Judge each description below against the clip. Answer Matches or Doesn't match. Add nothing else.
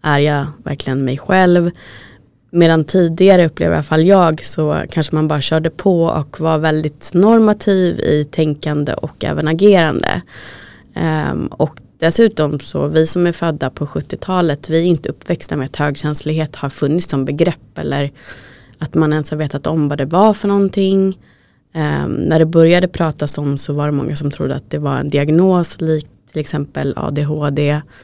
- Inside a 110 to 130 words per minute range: Doesn't match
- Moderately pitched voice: Matches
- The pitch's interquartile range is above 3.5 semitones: Doesn't match